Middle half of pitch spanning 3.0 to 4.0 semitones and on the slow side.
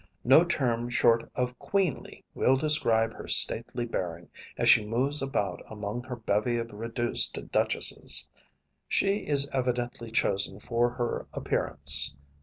Yes: average, 3.3 semitones; slow, 130 wpm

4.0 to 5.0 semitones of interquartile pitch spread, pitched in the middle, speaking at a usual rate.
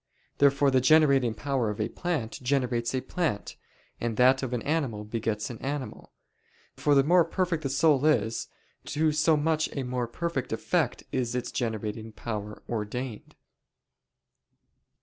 No: average, 4.4 semitones; low, 130 Hz; average, 150 wpm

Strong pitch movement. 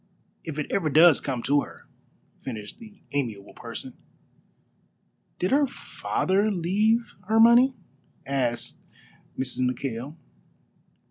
Yes: wide, 9.0 semitones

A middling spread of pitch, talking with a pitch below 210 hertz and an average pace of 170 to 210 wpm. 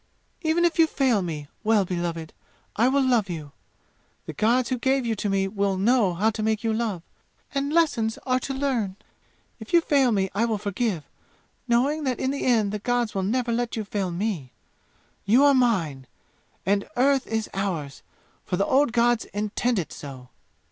No: average, 4.8 semitones; high, 220 Hz; average, 185 wpm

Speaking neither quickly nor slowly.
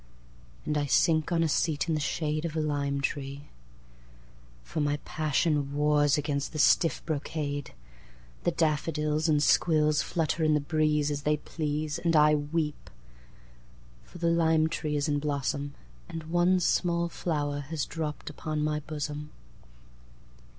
No: slow, 125 wpm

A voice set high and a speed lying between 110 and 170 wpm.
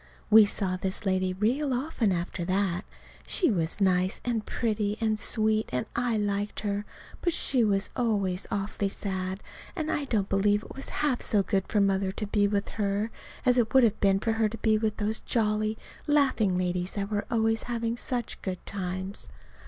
No: high, 210 Hz; average, 185 wpm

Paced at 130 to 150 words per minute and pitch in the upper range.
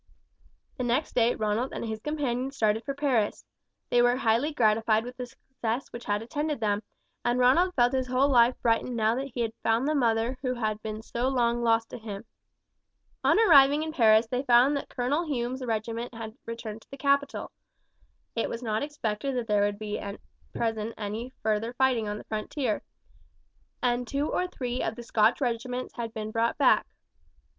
No: average, 185 wpm; high, 240 Hz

